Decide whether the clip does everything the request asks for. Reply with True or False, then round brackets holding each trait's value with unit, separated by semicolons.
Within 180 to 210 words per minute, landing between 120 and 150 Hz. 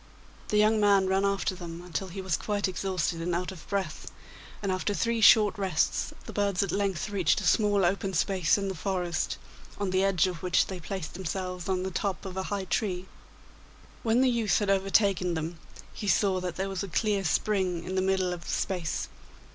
False (205 wpm; 190 Hz)